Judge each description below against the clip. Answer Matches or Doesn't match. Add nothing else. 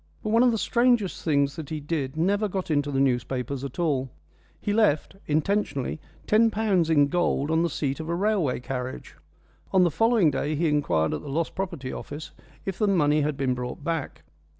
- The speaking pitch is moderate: Matches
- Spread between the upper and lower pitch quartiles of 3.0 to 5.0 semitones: Doesn't match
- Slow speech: Doesn't match